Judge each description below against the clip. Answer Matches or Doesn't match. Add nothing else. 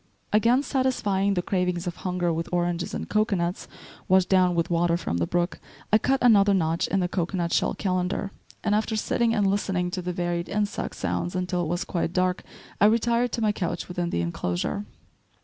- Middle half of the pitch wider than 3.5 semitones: Doesn't match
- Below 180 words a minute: Doesn't match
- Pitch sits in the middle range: Matches